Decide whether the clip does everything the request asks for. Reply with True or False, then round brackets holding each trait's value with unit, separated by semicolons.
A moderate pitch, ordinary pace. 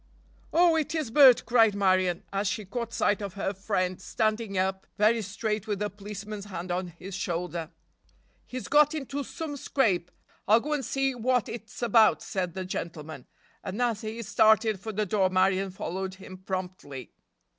False (205 Hz; 170 wpm)